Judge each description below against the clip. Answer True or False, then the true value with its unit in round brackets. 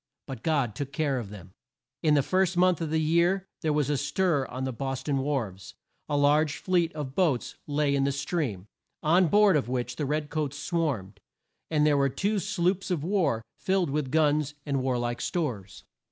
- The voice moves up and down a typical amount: True (4.0 semitones)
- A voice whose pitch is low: False (145 Hz)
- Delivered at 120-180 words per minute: False (195 wpm)